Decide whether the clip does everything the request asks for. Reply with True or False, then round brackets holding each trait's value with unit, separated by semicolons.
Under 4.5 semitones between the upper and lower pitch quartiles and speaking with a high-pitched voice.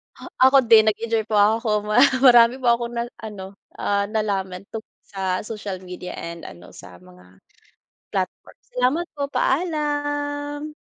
False (5.5 semitones; 220 Hz)